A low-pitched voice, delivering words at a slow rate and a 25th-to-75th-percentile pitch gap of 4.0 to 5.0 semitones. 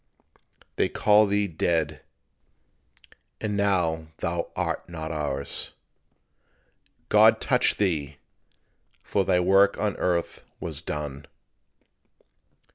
Yes: very low, 85 Hz; slow, 95 wpm; average, 4.4 semitones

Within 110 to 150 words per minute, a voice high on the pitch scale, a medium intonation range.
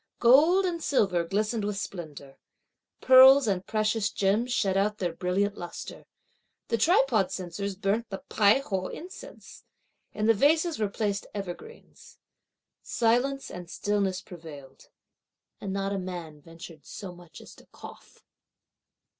Yes: slow, 135 wpm; high, 200 Hz; average, 4.5 semitones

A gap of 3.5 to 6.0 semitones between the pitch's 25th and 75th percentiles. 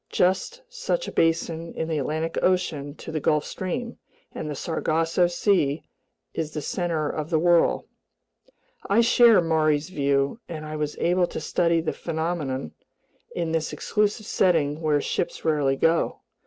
No: average, 2.8 semitones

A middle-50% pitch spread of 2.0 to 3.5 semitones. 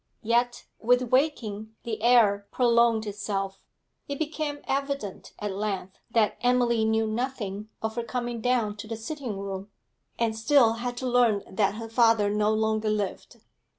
Yes: average, 2.8 semitones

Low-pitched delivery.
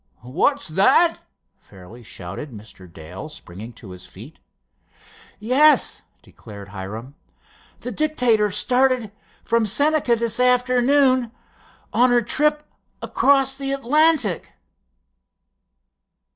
No: high, 235 Hz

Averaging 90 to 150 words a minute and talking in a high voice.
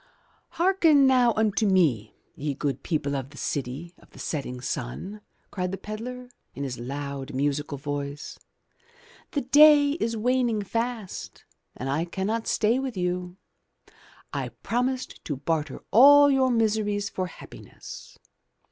Yes: average, 140 wpm; high, 195 Hz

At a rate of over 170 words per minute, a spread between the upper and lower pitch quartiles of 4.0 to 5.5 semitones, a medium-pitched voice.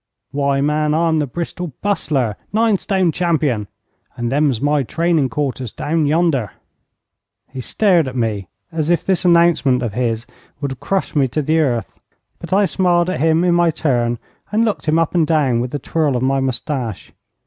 Yes: average, 180 wpm; average, 4.8 semitones; medium, 150 Hz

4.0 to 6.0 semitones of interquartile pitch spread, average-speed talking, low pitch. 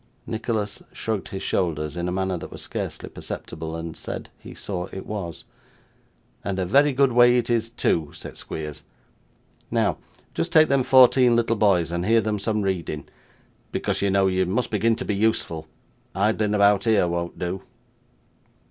Yes: average, 4.5 semitones; average, 170 wpm; low, 100 Hz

